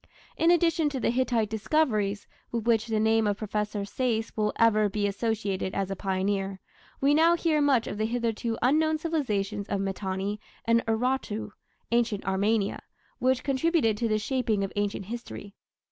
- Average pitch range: Yes, average, 3.9 semitones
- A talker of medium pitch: No, high, 220 Hz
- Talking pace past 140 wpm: Yes, average, 160 wpm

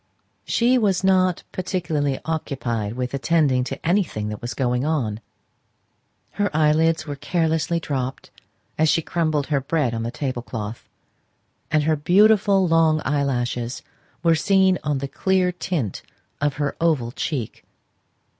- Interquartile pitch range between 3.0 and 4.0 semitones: No, average, 4.9 semitones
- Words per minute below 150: Yes, slow, 135 wpm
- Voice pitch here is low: No, medium, 150 Hz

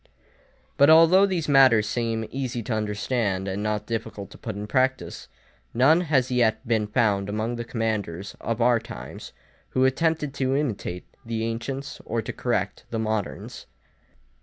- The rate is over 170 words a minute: No, average, 155 wpm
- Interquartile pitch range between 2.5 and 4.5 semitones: Yes, average, 3.7 semitones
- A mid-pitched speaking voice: No, low, 115 Hz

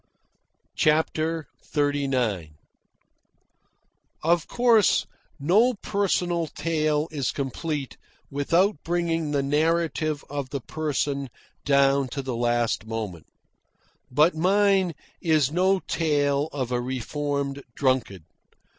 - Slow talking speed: Yes, slow, 95 wpm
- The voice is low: No, medium, 150 Hz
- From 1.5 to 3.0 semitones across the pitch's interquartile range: No, average, 3.4 semitones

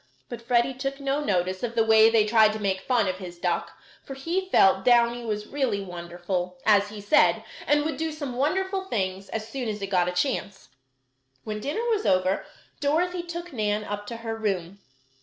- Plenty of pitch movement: Yes, wide, 5.9 semitones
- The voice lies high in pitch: Yes, high, 220 Hz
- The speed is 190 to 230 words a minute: Yes, average, 195 wpm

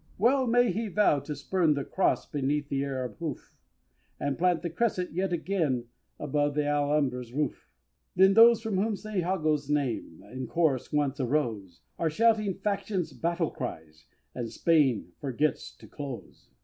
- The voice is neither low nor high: Yes, medium, 150 Hz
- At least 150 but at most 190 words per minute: Yes, average, 155 wpm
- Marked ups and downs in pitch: Yes, wide, 5.7 semitones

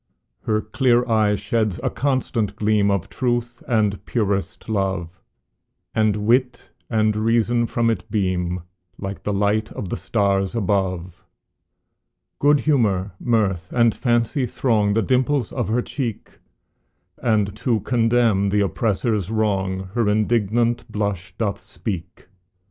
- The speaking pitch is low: Yes, low, 110 Hz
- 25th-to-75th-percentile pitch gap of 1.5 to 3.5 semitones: Yes, average, 3.1 semitones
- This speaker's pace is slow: Yes, slow, 125 wpm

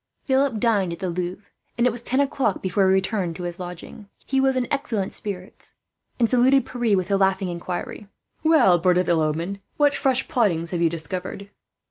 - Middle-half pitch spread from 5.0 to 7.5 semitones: Yes, wide, 5.6 semitones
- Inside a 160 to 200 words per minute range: Yes, average, 195 wpm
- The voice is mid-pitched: No, high, 195 Hz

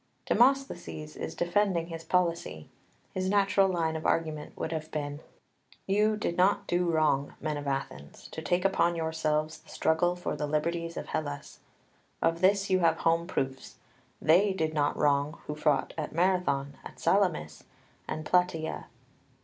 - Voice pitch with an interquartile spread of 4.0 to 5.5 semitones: No, average, 3.2 semitones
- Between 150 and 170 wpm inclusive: Yes, average, 155 wpm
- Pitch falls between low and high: Yes, medium, 165 Hz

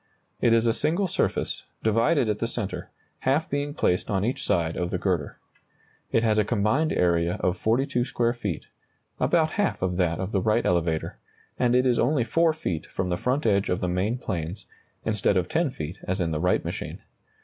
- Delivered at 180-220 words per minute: Yes, average, 200 wpm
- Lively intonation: Yes, wide, 5.8 semitones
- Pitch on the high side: No, low, 105 Hz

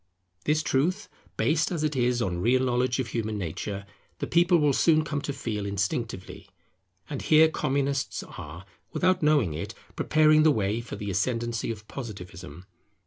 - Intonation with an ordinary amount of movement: No, wide, 6.9 semitones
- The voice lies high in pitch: No, low, 125 Hz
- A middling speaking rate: Yes, average, 160 wpm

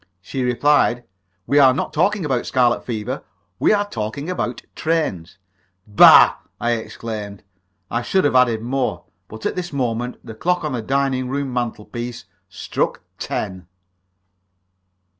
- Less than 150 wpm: Yes, average, 140 wpm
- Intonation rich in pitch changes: No, average, 4.1 semitones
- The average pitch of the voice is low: Yes, low, 125 Hz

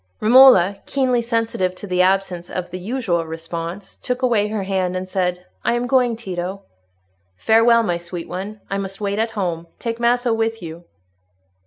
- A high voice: Yes, high, 195 Hz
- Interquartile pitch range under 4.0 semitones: No, average, 4.3 semitones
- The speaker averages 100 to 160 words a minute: No, average, 170 wpm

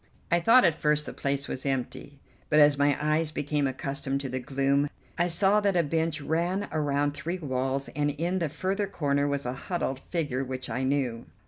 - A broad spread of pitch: No, average, 3.3 semitones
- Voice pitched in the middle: Yes, medium, 145 Hz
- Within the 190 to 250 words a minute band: Yes, average, 200 wpm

